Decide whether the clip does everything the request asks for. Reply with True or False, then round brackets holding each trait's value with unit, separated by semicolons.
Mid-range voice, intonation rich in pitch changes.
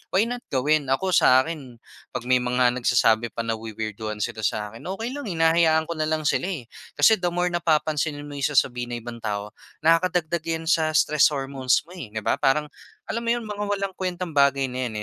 True (150 Hz; 6.0 semitones)